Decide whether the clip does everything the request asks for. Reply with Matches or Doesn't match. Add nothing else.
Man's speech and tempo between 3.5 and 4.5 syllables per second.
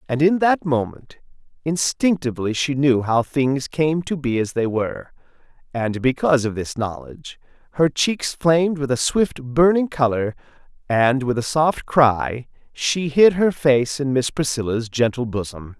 Matches